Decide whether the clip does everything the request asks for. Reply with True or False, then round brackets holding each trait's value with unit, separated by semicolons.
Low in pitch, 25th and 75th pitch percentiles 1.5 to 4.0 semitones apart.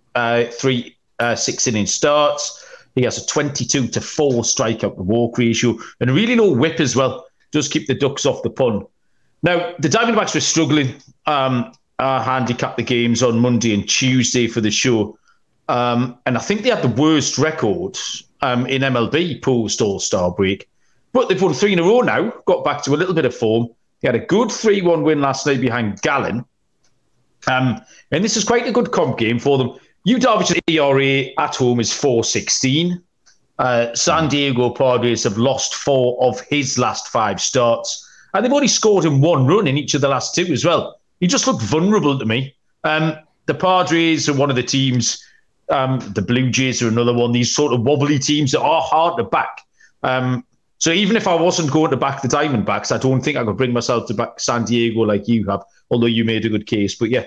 False (130 Hz; 4.7 semitones)